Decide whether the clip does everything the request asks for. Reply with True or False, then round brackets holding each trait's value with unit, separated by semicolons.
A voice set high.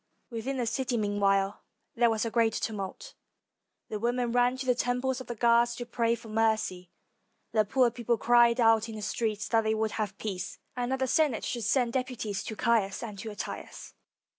True (230 Hz)